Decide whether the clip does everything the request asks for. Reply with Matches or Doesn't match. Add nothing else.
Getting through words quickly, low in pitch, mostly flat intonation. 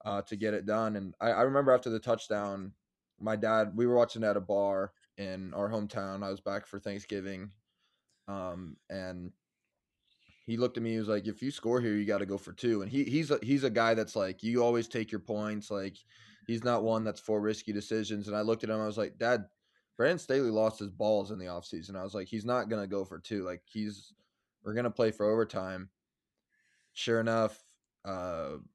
Matches